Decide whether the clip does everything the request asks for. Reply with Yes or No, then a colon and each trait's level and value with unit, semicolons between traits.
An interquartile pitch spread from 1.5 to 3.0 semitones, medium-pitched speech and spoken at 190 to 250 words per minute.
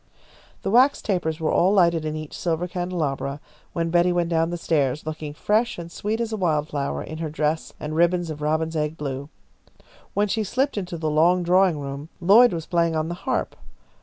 Yes: average, 2.7 semitones; medium, 165 Hz; average, 195 wpm